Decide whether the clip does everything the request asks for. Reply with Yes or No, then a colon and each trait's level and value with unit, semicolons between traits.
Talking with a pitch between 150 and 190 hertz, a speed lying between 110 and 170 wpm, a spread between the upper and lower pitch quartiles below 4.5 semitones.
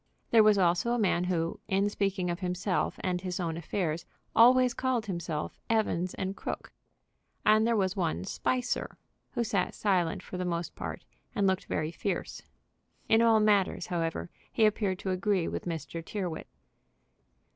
Yes: medium, 185 Hz; average, 160 wpm; average, 3.7 semitones